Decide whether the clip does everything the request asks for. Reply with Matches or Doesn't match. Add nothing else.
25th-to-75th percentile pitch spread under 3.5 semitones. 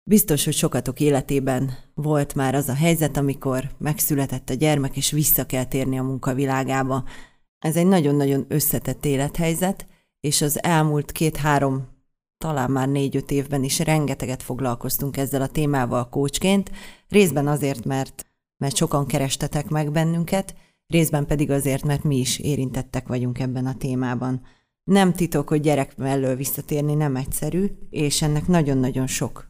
Matches